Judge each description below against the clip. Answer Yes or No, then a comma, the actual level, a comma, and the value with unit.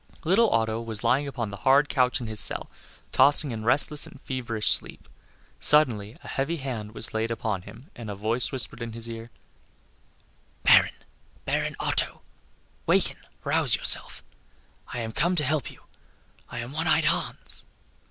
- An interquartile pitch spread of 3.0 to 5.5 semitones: Yes, average, 3.9 semitones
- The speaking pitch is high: No, low, 120 Hz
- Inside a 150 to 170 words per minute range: Yes, average, 160 wpm